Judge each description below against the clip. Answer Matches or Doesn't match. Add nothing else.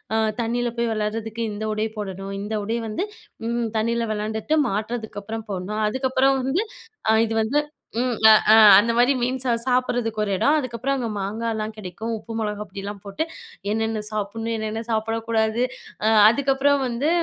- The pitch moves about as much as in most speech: Doesn't match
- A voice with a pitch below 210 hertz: Doesn't match